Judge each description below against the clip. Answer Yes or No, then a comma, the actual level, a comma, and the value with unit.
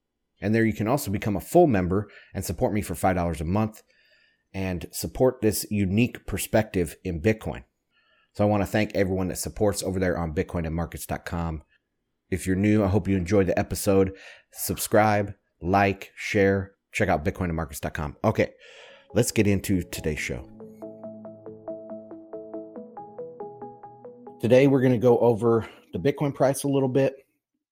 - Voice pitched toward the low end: Yes, low, 105 Hz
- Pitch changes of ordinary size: Yes, average, 3.3 semitones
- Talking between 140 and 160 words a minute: Yes, average, 145 wpm